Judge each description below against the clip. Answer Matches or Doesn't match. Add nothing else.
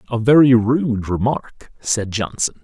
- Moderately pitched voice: Doesn't match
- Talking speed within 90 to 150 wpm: Matches